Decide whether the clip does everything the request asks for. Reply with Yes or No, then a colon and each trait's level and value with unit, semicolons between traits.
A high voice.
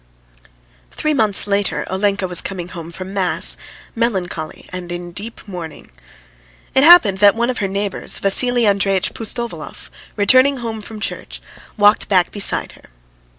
Yes: high, 200 Hz